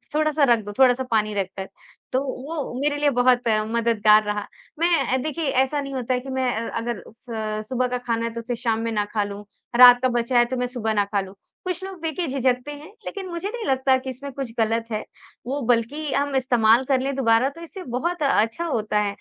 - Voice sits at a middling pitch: No, very high, 250 Hz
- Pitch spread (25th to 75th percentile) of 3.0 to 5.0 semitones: Yes, average, 3.7 semitones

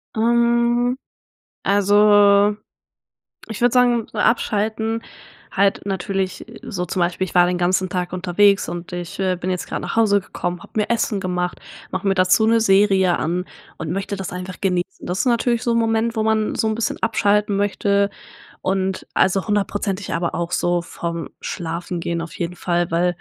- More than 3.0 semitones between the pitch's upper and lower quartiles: Yes, average, 3.4 semitones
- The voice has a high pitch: Yes, high, 195 Hz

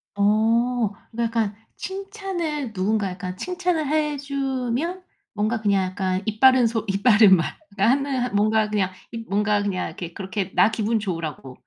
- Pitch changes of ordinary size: Yes, average, 4.9 semitones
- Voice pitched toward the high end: Yes, high, 220 Hz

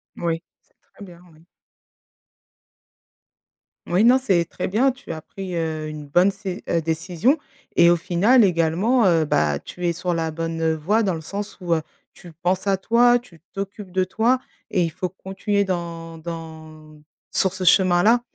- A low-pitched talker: No, medium, 175 Hz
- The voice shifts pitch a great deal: No, average, 3.3 semitones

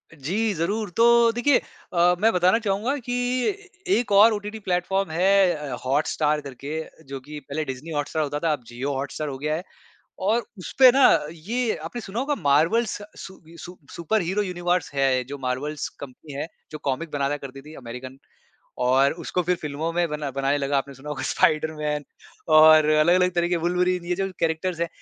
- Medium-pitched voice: Yes, medium, 160 Hz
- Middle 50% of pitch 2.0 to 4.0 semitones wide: No, average, 5.2 semitones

